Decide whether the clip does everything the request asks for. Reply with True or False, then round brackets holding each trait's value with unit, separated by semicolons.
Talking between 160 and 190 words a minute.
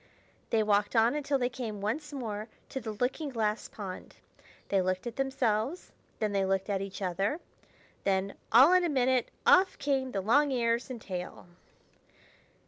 True (165 wpm)